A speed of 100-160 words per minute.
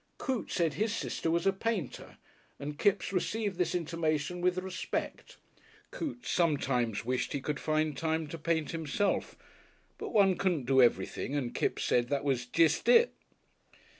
Yes: average, 155 wpm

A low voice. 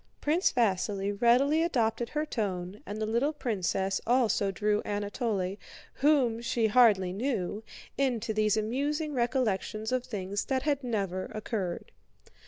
No: high, 220 Hz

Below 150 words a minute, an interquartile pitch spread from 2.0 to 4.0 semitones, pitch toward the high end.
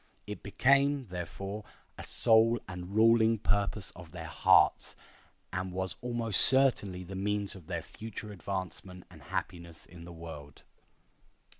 No: slow, 135 wpm; average, 3.7 semitones; low, 100 Hz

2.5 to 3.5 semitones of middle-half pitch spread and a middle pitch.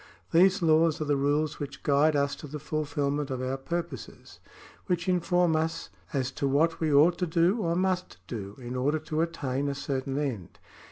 Yes: average, 3.2 semitones; medium, 150 Hz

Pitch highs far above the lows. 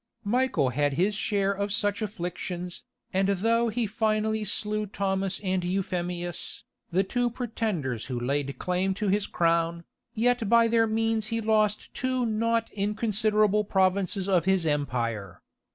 No: average, 3.6 semitones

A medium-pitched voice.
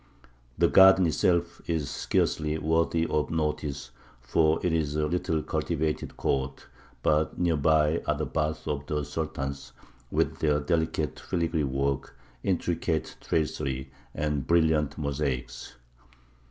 No: very low, 75 Hz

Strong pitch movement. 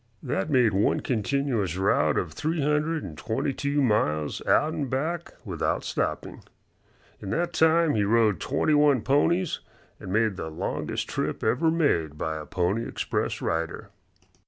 Yes: wide, 8.0 semitones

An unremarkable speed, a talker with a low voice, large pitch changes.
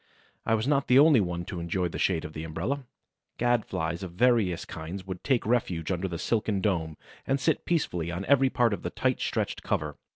No: fast, 215 wpm; very low, 95 Hz; wide, 6.3 semitones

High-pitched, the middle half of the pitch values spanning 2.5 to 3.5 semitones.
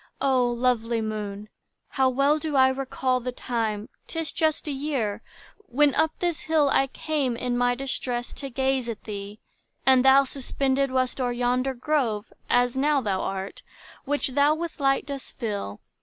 Yes: very high, 260 Hz; average, 2.8 semitones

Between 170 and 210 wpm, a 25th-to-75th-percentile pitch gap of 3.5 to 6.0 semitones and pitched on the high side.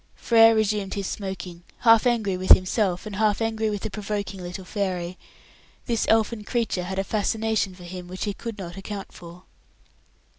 No: average, 175 wpm; average, 2.9 semitones; high, 200 Hz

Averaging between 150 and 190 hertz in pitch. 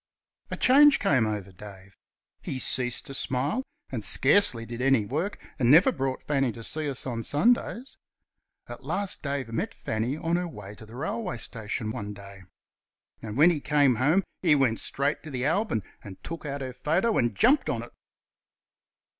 No: low, 135 Hz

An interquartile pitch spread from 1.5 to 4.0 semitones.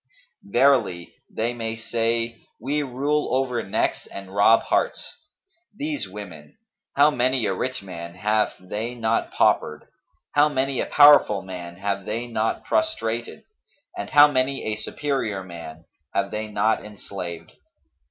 No: average, 5.1 semitones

